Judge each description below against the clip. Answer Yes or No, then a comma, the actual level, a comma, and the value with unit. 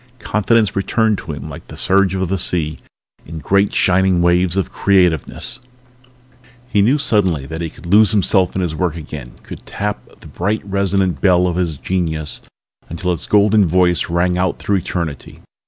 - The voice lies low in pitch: Yes, very low, 90 Hz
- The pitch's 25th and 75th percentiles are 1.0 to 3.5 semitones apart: Yes, narrow, 2.6 semitones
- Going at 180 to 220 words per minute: No, average, 170 wpm